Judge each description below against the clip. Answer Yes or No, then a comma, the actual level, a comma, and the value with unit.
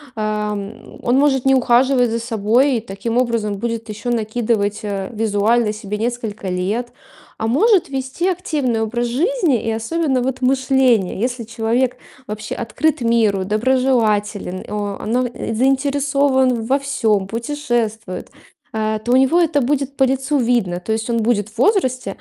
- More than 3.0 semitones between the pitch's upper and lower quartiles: Yes, average, 3.6 semitones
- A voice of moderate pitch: No, high, 235 Hz